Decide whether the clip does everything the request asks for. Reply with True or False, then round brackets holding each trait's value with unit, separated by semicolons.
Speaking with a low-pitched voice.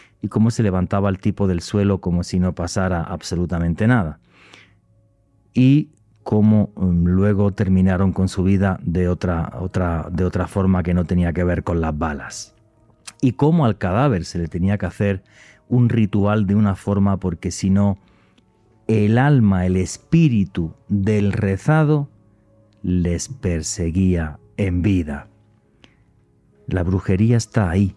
True (100 Hz)